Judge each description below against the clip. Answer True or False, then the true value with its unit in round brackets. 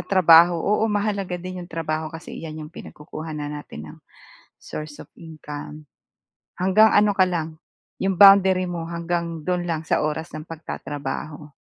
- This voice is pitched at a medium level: True (165 Hz)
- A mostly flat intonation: False (3.1 semitones)